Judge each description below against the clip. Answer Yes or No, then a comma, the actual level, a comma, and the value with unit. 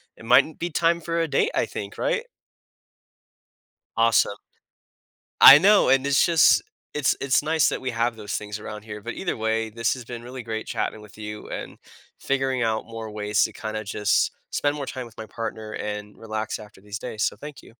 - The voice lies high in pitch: No, low, 115 Hz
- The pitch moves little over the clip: No, average, 4.2 semitones